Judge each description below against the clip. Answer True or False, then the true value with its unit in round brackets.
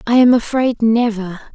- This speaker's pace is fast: False (155 wpm)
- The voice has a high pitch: True (230 Hz)